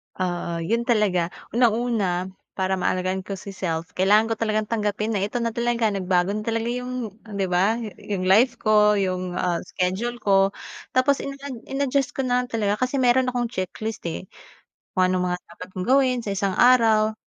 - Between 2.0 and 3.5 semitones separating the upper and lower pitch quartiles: No, average, 4.4 semitones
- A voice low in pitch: No, high, 215 Hz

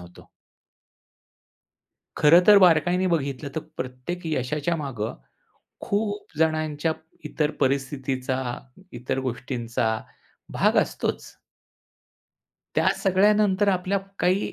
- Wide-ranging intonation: Yes, wide, 5.8 semitones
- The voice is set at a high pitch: No, medium, 150 Hz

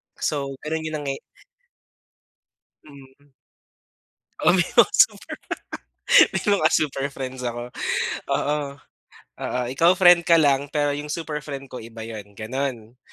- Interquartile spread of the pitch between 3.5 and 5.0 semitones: No, average, 3.1 semitones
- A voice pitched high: No, medium, 140 Hz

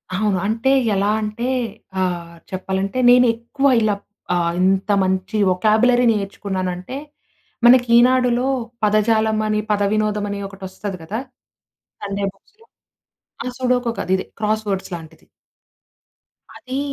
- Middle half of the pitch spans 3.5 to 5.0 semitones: Yes, average, 3.9 semitones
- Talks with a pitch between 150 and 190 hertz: No, high, 210 Hz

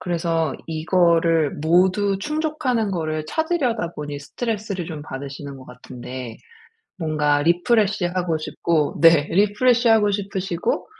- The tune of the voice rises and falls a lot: No, average, 4.9 semitones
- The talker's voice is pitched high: No, medium, 175 Hz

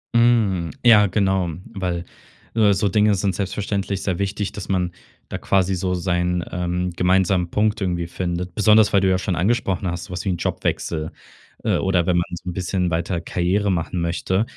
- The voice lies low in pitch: Yes, very low, 95 Hz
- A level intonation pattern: Yes, narrow, 2.3 semitones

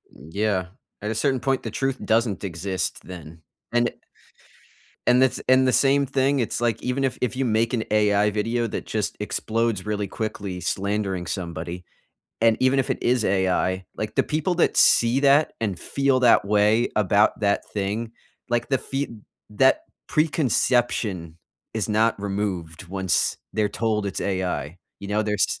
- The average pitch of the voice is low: Yes, low, 110 Hz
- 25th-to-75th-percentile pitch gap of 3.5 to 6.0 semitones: Yes, average, 4.2 semitones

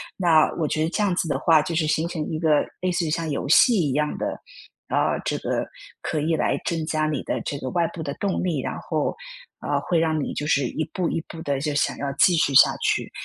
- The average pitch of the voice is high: No, medium, 160 Hz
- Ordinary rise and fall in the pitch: No, narrow, 2.3 semitones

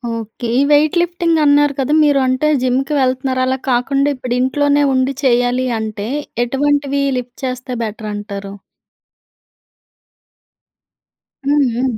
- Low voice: No, very high, 260 Hz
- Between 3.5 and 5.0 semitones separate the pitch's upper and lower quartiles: No, average, 2.8 semitones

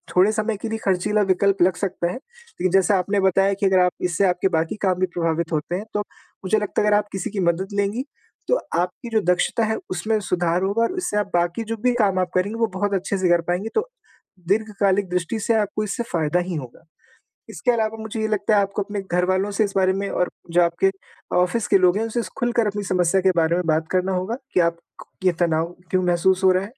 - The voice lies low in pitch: No, high, 195 Hz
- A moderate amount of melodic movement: Yes, average, 3.0 semitones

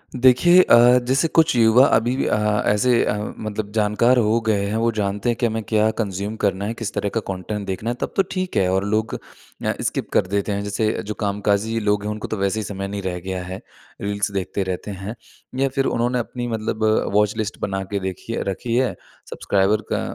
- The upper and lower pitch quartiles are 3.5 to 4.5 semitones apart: No, average, 2.7 semitones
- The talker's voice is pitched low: Yes, low, 105 Hz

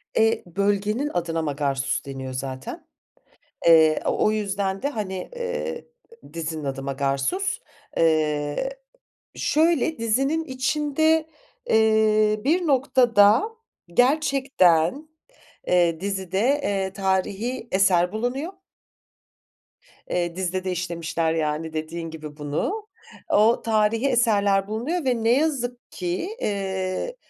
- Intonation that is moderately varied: No, wide, 7.6 semitones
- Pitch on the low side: No, high, 200 Hz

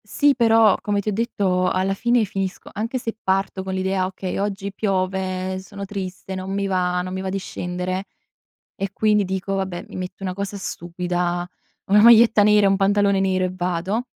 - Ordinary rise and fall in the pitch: No, narrow, 1.7 semitones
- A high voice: Yes, high, 195 Hz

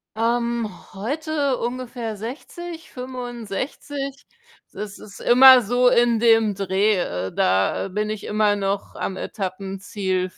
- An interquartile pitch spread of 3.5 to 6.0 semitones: Yes, average, 4.2 semitones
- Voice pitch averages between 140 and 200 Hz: No, high, 225 Hz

